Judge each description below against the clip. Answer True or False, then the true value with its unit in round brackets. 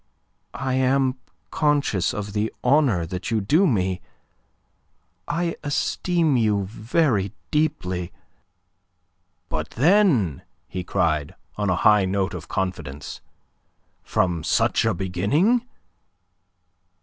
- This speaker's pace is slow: True (100 wpm)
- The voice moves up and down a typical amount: False (8.0 semitones)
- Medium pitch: False (105 Hz)